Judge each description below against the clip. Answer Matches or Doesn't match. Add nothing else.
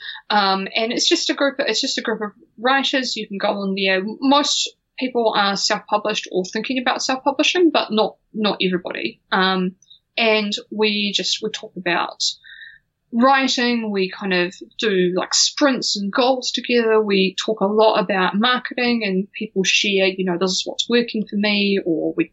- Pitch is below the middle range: Doesn't match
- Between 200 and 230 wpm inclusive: Doesn't match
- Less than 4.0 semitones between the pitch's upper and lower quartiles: Doesn't match